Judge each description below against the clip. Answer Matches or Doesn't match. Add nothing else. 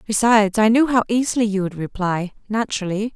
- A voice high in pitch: Matches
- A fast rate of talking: Doesn't match